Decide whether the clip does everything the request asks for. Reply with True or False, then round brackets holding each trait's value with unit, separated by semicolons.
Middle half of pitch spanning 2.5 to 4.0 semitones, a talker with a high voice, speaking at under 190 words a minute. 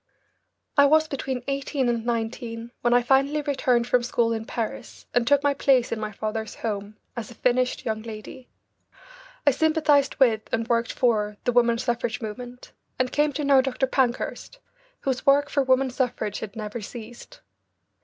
True (3.0 semitones; 245 Hz; 170 wpm)